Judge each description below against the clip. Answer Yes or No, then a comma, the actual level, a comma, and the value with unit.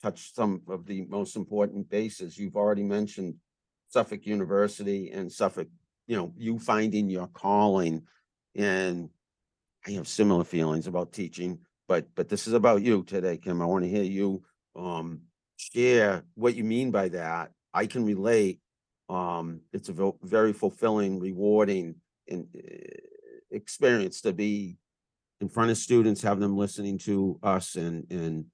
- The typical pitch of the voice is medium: No, low, 100 Hz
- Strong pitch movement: No, average, 2.7 semitones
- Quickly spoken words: No, average, 145 wpm